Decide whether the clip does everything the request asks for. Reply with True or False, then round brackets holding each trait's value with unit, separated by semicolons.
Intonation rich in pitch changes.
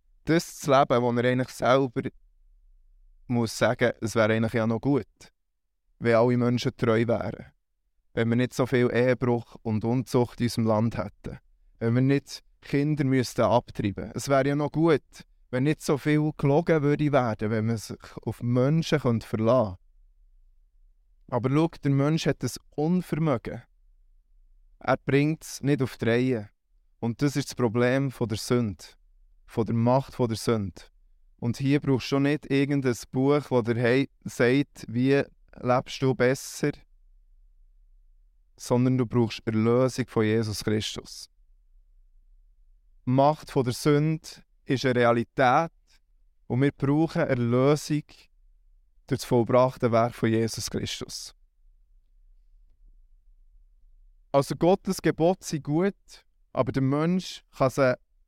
True (8.0 semitones)